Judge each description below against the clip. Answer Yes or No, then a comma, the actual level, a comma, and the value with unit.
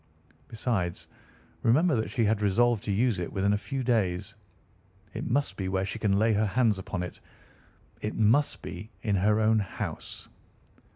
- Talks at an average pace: Yes, average, 170 wpm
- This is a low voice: Yes, low, 105 Hz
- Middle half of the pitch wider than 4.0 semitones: No, average, 3.0 semitones